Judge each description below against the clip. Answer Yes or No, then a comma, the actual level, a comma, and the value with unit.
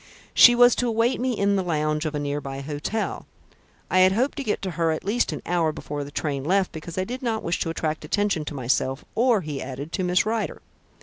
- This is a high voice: No, medium, 175 Hz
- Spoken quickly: Yes, fast, 240 wpm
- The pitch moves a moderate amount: No, wide, 6.5 semitones